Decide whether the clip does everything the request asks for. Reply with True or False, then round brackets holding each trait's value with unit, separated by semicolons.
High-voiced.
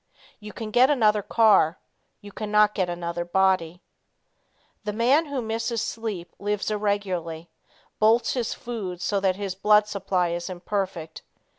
True (205 Hz)